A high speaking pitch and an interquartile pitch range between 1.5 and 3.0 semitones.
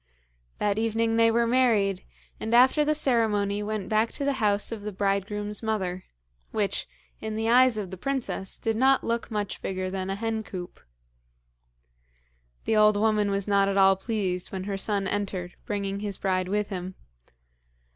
Yes: high, 210 Hz; narrow, 2.5 semitones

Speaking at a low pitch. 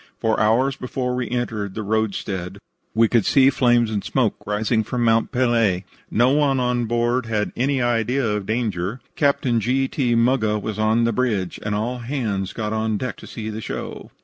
Yes: low, 115 Hz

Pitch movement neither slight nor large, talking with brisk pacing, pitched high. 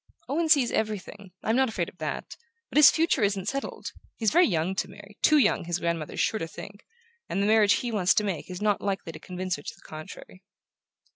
Yes: average, 3.7 semitones; fast, 225 wpm; high, 200 Hz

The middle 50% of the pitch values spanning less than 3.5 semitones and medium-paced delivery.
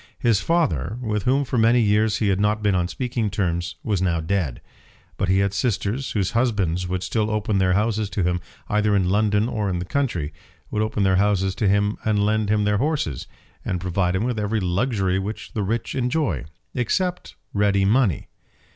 Yes: average, 3.0 semitones; average, 195 wpm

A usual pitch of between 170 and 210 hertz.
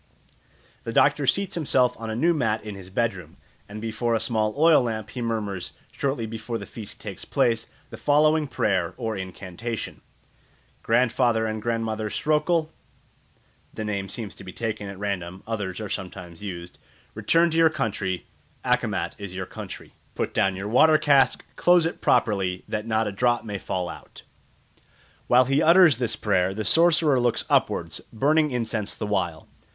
No: low, 110 Hz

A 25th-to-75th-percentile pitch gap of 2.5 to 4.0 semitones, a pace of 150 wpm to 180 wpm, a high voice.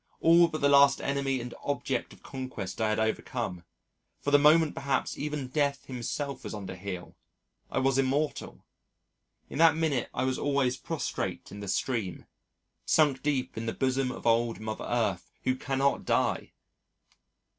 No: average, 3.5 semitones; average, 160 wpm; low, 130 Hz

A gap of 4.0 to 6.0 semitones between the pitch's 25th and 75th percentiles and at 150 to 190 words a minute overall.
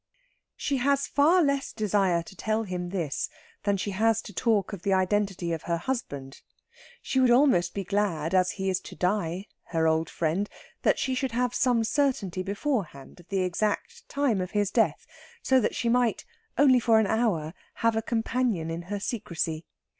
Yes: average, 5.3 semitones; average, 180 wpm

